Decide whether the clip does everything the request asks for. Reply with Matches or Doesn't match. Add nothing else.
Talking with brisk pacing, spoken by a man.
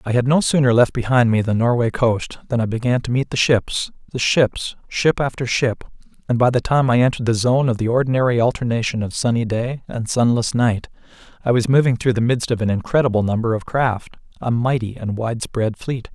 Matches